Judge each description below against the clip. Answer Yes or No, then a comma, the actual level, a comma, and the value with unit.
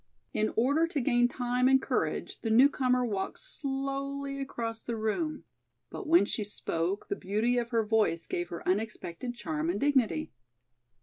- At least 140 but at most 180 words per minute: Yes, average, 160 wpm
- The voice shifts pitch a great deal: No, average, 4.7 semitones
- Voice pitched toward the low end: No, high, 240 Hz